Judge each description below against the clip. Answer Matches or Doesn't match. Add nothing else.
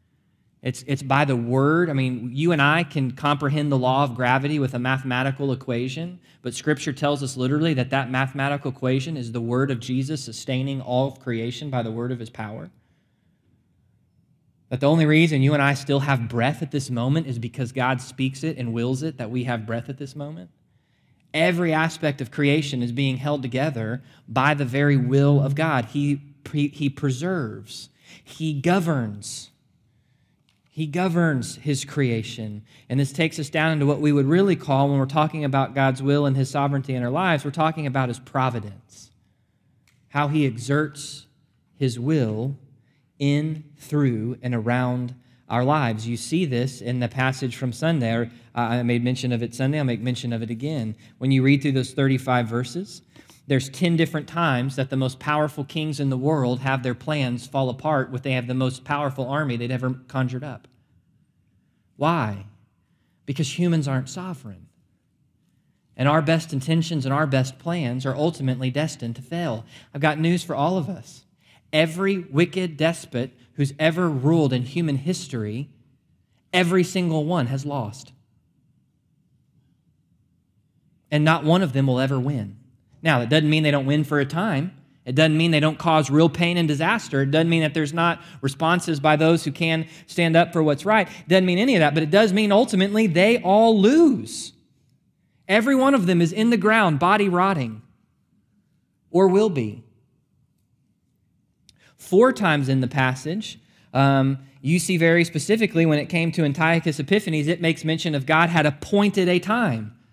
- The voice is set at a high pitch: Doesn't match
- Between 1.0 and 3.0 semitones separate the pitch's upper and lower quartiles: Doesn't match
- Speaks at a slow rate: Doesn't match